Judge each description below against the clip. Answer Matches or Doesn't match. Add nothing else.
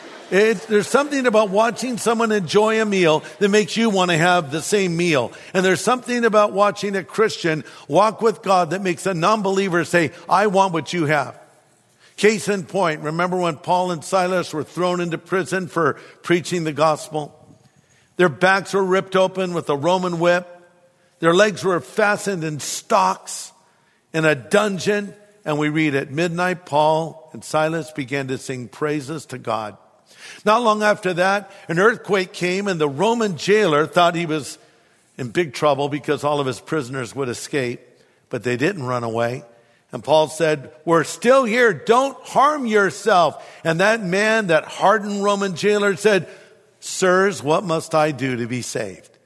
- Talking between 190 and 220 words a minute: Doesn't match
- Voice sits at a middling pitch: Matches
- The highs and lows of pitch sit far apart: Doesn't match